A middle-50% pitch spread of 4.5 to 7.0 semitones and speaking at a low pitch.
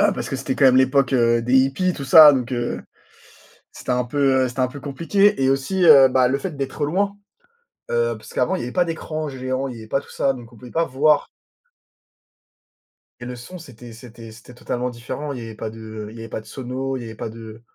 No: average, 2.9 semitones; low, 130 Hz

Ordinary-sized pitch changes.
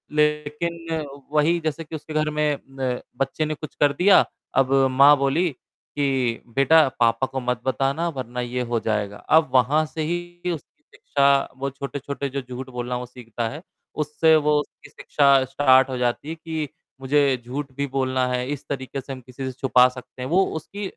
Yes: average, 3.1 semitones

